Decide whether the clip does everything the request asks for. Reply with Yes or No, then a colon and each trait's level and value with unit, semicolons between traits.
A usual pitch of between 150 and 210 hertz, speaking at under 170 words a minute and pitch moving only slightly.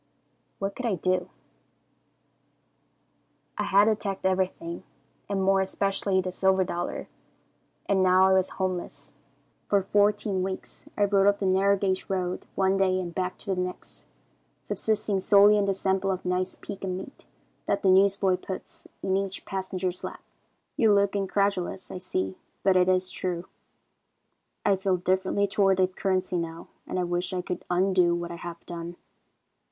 Yes: high, 190 Hz; average, 160 wpm; narrow, 1.4 semitones